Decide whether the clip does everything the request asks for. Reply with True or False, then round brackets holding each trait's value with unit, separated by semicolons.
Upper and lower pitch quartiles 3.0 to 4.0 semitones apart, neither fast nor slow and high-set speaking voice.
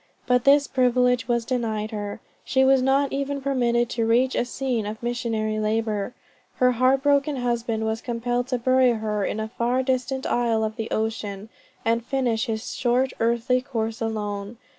False (2.5 semitones; 170 wpm; 240 Hz)